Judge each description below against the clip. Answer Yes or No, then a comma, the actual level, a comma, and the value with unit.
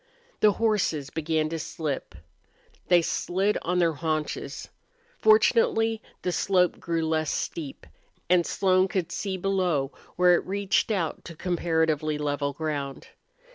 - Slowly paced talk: Yes, slow, 130 wpm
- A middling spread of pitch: Yes, average, 3.3 semitones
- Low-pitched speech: No, medium, 170 Hz